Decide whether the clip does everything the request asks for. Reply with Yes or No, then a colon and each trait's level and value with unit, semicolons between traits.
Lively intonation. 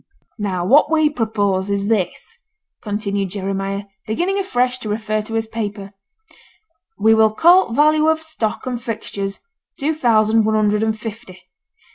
No: average, 3.8 semitones